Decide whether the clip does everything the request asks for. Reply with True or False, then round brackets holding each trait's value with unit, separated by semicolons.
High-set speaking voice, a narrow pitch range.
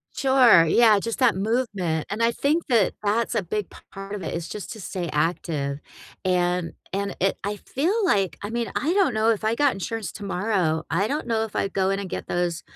False (205 Hz; 4.3 semitones)